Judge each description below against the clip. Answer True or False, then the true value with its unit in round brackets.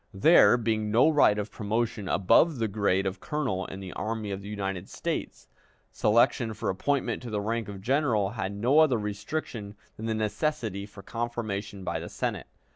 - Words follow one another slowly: False (180 wpm)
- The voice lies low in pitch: True (110 Hz)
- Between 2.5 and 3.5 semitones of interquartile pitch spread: True (2.9 semitones)